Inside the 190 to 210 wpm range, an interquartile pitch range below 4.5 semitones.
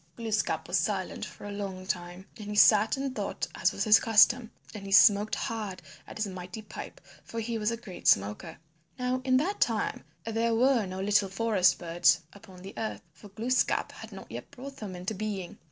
Yes: average, 200 wpm; average, 3.3 semitones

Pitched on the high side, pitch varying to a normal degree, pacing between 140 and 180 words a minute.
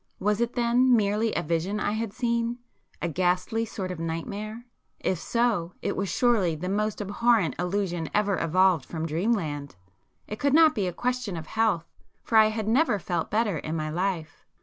Yes: high, 200 Hz; average, 4.9 semitones; average, 175 wpm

